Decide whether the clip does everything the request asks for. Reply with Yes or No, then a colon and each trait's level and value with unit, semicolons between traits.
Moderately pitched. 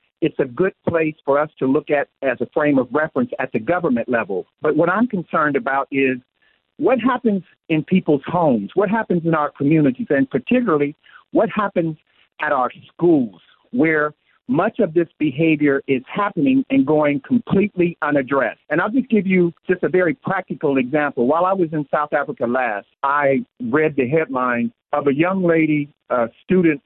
Yes: medium, 160 Hz